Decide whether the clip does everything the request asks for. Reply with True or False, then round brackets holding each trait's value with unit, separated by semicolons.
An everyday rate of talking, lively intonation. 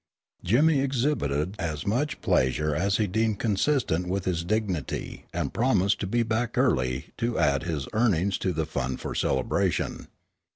True (155 wpm; 6.9 semitones)